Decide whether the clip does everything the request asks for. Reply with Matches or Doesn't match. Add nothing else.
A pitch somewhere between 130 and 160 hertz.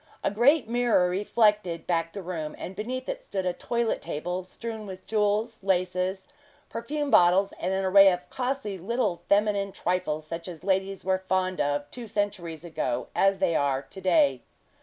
Doesn't match